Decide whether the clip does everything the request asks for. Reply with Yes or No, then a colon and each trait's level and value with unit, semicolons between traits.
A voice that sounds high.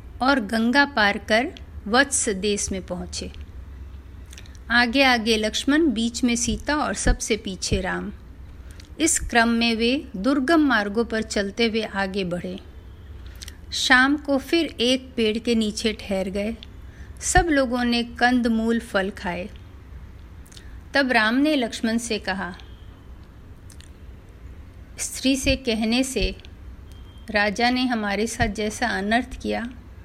Yes: high, 215 Hz